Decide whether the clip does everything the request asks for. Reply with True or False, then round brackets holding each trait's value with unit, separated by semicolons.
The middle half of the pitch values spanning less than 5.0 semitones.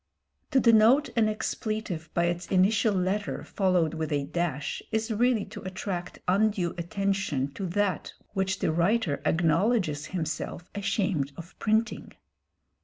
True (4.0 semitones)